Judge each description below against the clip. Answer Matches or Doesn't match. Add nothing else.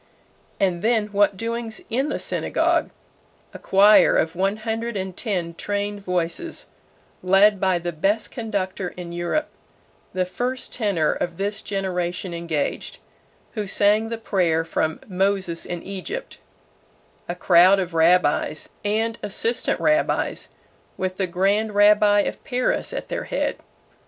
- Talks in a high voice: Matches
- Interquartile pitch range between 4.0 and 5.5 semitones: Doesn't match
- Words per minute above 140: Doesn't match